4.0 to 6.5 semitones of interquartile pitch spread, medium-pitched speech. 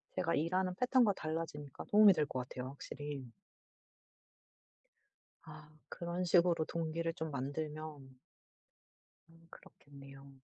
No: average, 3.3 semitones; medium, 155 Hz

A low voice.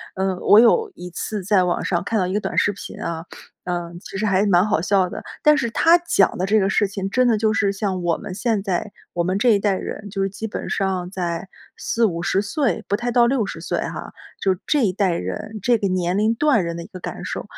No: high, 195 Hz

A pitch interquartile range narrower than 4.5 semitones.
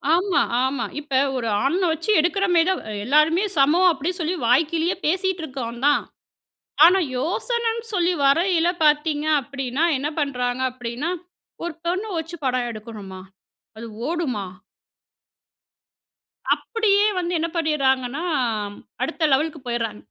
No: average, 5.0 semitones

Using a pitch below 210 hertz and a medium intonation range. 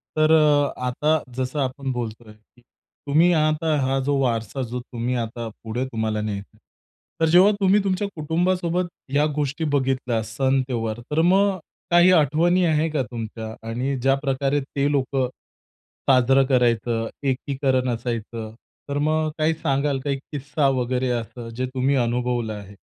Yes: low, 135 Hz; average, 4.3 semitones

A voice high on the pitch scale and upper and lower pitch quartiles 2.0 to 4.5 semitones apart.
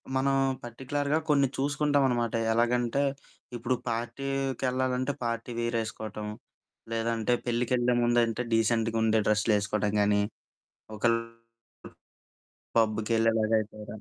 No: low, 115 Hz; narrow, 2.5 semitones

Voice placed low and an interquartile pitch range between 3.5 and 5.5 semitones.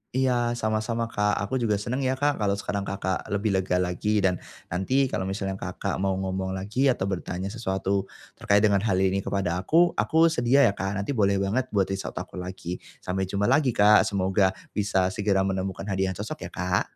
No: low, 100 Hz; average, 3.1 semitones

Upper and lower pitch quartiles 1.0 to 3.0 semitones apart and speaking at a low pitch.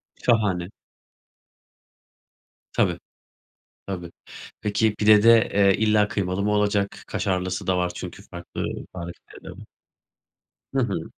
Yes: narrow, 2.5 semitones; low, 100 Hz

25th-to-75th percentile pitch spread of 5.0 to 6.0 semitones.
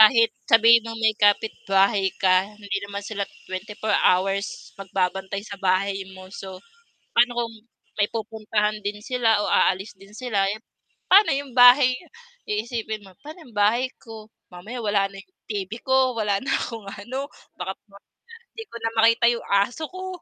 No: average, 3.0 semitones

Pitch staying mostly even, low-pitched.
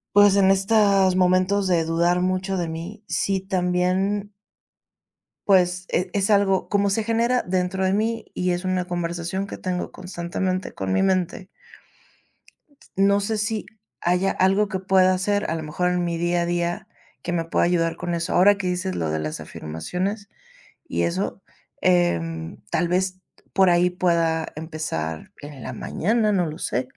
No: narrow, 2.2 semitones; medium, 185 Hz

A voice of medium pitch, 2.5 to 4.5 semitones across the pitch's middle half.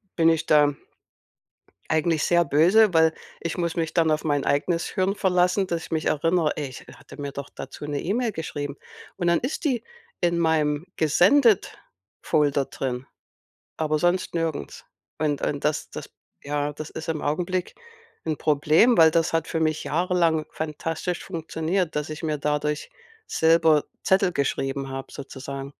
Yes: medium, 160 Hz; average, 2.8 semitones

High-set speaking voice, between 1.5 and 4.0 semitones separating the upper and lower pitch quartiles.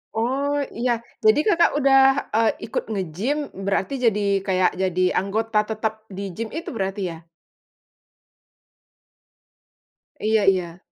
No: high, 215 Hz; average, 4.5 semitones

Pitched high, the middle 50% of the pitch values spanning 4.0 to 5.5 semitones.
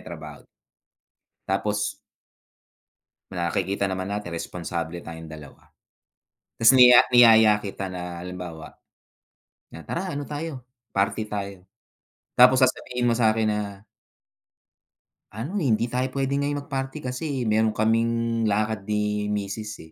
No: low, 105 Hz; average, 4.3 semitones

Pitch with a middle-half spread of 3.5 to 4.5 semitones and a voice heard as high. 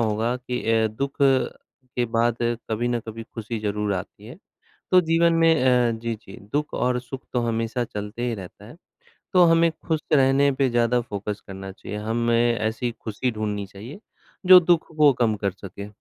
No: average, 3.8 semitones; low, 120 Hz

